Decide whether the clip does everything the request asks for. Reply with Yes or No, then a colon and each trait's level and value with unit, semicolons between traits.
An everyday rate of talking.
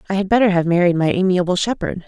No: fast, 230 wpm